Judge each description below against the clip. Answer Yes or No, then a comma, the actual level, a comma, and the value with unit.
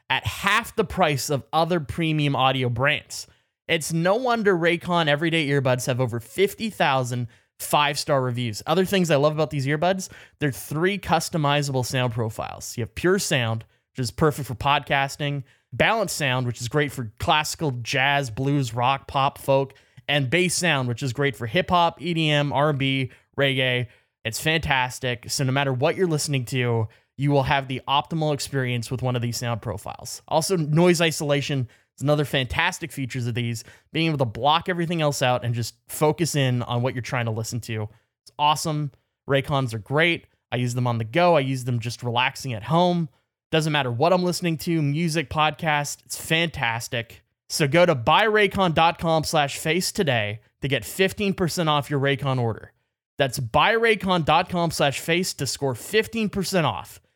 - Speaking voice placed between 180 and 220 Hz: No, medium, 140 Hz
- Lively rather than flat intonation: No, average, 4.7 semitones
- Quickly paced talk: No, average, 170 wpm